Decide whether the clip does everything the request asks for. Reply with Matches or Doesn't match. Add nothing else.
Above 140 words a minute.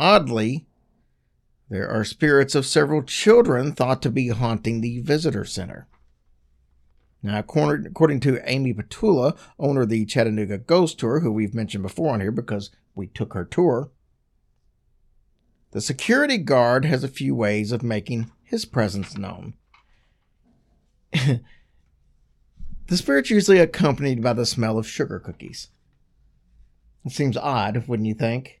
Doesn't match